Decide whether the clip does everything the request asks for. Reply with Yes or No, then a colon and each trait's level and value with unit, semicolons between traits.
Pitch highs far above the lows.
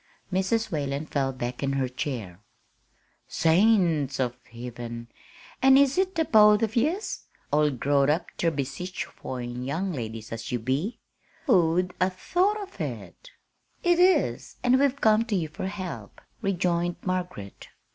Yes: wide, 8.7 semitones